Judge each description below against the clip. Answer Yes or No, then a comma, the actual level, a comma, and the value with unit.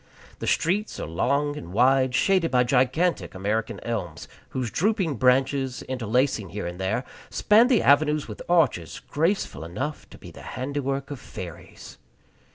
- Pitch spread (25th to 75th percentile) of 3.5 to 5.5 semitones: Yes, average, 5.2 semitones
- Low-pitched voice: Yes, low, 130 Hz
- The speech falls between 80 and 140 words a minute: No, average, 150 wpm